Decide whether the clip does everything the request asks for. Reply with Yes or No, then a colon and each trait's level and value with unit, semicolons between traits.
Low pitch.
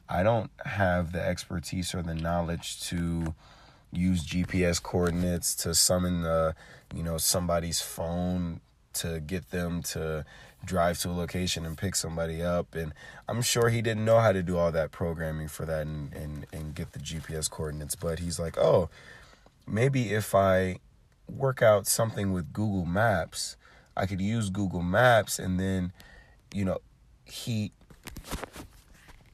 Yes: very low, 85 Hz